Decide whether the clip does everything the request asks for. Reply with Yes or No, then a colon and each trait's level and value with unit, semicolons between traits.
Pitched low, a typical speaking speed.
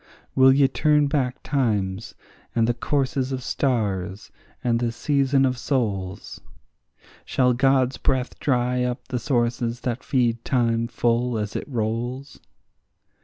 No: low, 125 Hz; slow, 130 wpm